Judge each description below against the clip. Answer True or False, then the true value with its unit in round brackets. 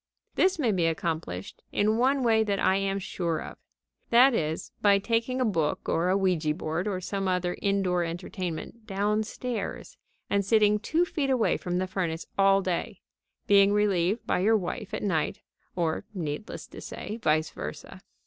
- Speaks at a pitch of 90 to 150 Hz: False (195 Hz)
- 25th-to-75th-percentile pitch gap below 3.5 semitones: False (3.8 semitones)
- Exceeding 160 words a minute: True (170 wpm)